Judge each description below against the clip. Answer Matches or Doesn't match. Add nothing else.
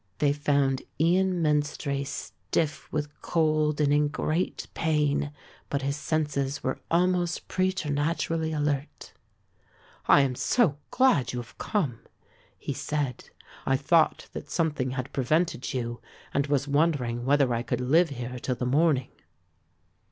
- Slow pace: Matches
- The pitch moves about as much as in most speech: Matches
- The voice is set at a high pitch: Doesn't match